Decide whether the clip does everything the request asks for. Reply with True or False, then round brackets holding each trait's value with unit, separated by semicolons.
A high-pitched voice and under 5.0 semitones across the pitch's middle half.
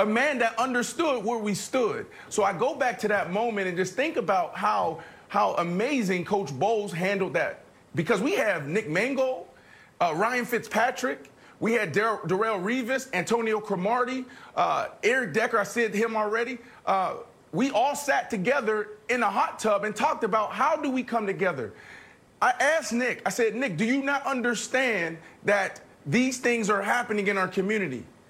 True (225 Hz; 3.7 semitones)